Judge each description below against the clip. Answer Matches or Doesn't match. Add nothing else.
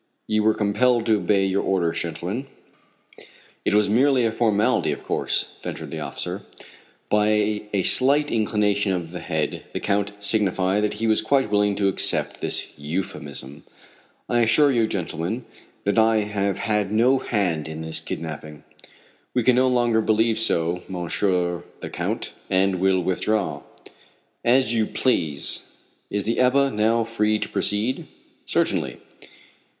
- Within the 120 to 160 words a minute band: Matches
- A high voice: Doesn't match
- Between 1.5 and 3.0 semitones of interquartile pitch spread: Doesn't match